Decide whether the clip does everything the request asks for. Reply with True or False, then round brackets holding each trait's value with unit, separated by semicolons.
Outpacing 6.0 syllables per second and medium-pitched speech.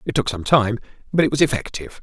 False (7.0 syllables/s; 125 Hz)